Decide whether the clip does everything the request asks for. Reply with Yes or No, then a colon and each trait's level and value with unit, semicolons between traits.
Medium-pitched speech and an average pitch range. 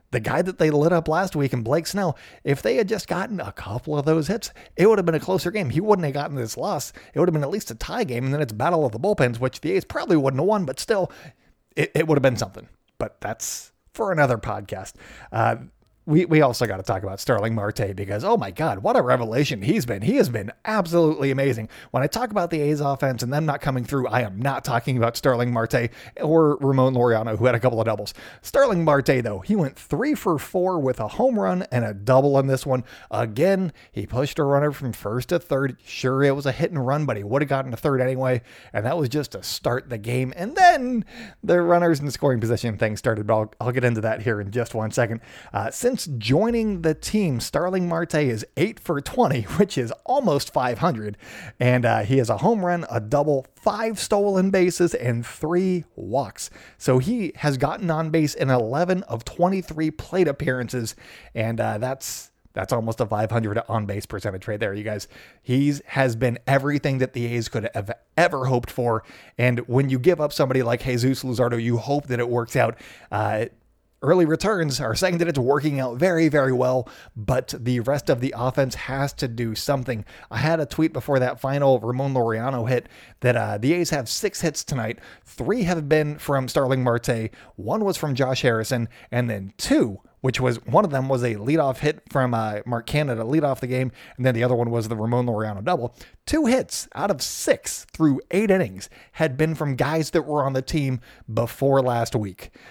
No: low, 130 Hz; average, 4.8 semitones